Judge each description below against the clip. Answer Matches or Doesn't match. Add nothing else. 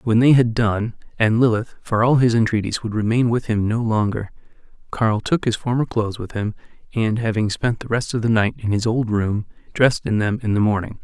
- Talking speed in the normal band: Doesn't match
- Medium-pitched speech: Doesn't match